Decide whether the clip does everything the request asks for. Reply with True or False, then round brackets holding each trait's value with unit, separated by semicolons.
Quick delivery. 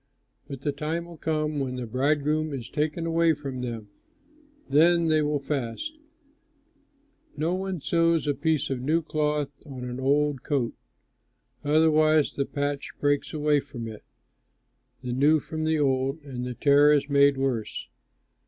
False (155 wpm)